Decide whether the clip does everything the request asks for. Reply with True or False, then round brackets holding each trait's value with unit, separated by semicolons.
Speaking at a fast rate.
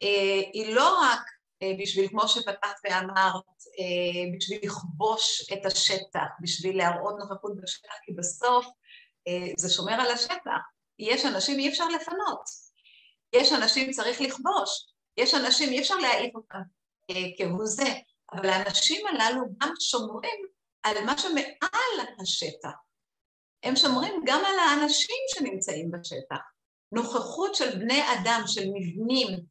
False (130 wpm)